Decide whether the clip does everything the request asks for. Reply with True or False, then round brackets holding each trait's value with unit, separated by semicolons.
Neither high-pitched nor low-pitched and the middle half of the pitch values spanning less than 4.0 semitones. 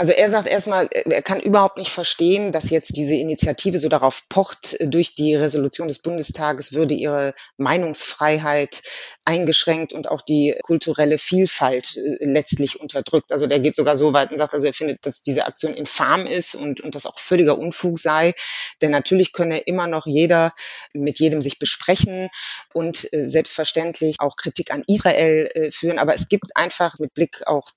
True (155 Hz; 2.5 semitones)